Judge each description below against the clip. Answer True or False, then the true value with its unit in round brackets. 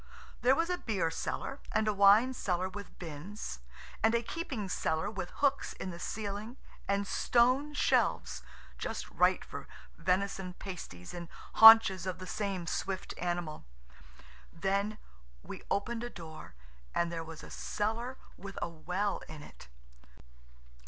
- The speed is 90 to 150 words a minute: True (140 wpm)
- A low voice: False (200 Hz)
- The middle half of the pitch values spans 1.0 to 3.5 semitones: False (4.4 semitones)